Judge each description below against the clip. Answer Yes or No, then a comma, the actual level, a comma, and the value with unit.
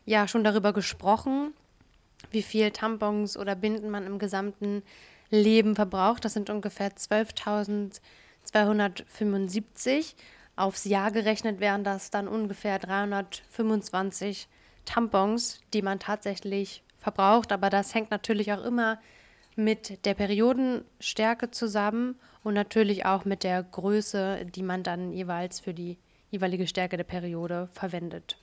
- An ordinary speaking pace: No, slow, 120 wpm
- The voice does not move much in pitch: Yes, narrow, 1.9 semitones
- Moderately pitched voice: No, high, 205 Hz